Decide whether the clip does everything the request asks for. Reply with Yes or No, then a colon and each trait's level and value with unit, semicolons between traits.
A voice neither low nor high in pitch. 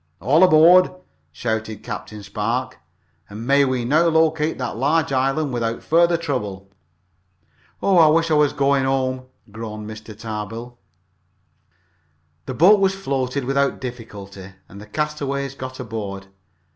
No: low, 130 Hz